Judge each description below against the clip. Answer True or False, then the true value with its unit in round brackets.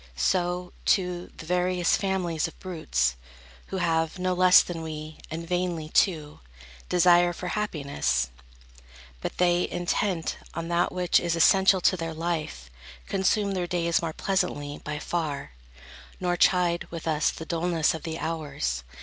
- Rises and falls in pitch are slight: True (2.1 semitones)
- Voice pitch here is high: False (170 Hz)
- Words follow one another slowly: False (145 wpm)